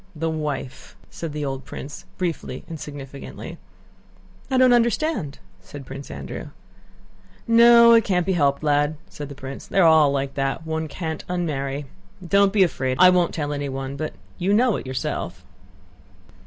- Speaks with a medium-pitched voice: Yes, medium, 155 Hz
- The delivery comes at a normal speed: Yes, average, 155 wpm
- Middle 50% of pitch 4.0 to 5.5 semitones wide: Yes, average, 4.7 semitones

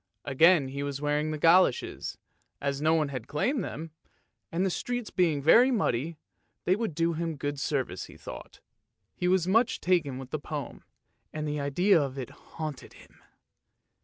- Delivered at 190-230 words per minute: No, average, 170 wpm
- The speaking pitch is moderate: Yes, medium, 155 Hz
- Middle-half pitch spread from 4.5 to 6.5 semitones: No, average, 4.1 semitones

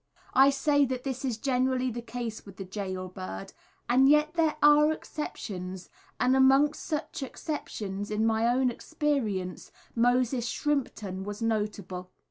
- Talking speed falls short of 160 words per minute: Yes, average, 140 wpm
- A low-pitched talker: No, high, 245 Hz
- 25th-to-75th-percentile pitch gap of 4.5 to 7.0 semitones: Yes, average, 5.2 semitones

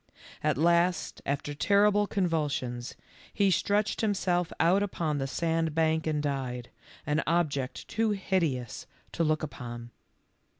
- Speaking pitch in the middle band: Yes, medium, 160 Hz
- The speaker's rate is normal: No, slow, 120 wpm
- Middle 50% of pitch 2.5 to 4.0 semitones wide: No, average, 4.8 semitones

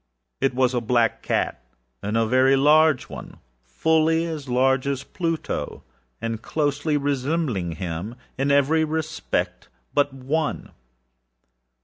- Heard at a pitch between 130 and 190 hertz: Yes, low, 135 Hz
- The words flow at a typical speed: No, slow, 105 wpm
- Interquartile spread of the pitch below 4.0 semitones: No, average, 5.1 semitones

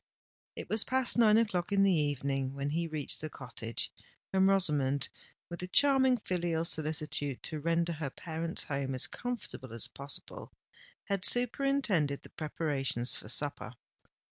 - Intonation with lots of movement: Yes, wide, 5.8 semitones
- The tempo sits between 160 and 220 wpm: No, average, 145 wpm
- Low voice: No, medium, 160 Hz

